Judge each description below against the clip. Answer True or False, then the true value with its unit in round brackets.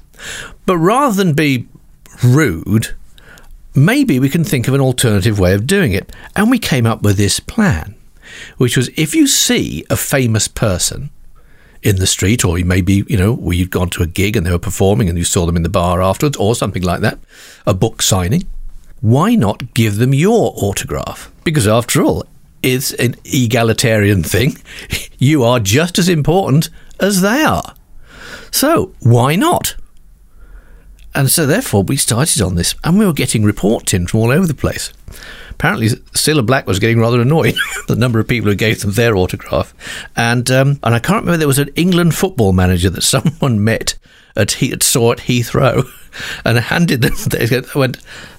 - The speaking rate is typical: True (180 wpm)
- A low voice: True (120 Hz)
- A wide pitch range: True (6.4 semitones)